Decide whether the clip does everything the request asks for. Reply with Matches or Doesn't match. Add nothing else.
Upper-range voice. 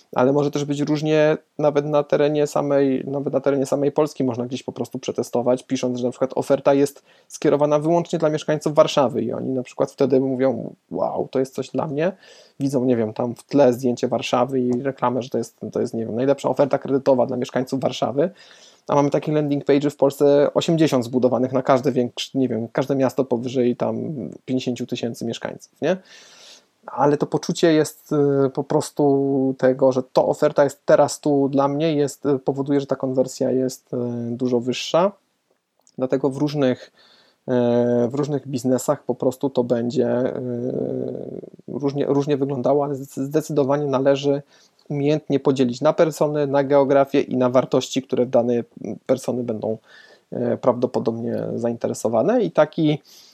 Doesn't match